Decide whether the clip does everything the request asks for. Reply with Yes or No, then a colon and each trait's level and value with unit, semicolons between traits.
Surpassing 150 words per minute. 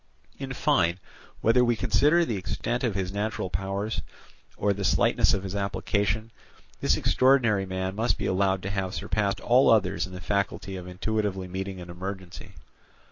Yes: average, 165 wpm